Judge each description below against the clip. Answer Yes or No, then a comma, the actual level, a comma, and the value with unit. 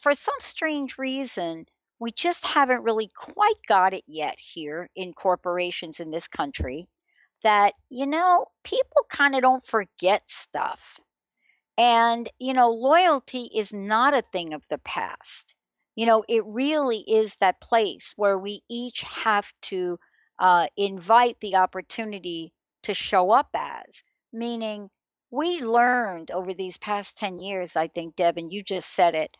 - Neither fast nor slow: Yes, average, 150 wpm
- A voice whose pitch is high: Yes, high, 220 Hz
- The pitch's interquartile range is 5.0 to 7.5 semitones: Yes, wide, 5.5 semitones